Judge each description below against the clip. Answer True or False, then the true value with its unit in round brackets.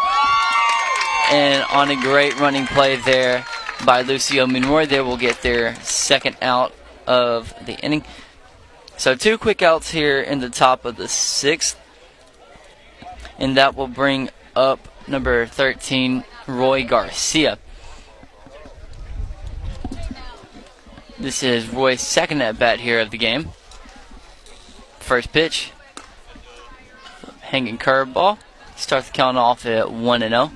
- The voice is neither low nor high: False (130 Hz)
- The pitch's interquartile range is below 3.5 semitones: True (2.7 semitones)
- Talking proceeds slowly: True (120 wpm)